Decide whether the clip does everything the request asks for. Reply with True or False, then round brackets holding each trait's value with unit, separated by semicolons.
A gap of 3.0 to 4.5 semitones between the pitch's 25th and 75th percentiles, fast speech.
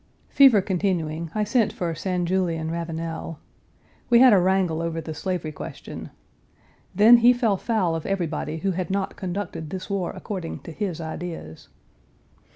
False (3.4 semitones; 155 wpm)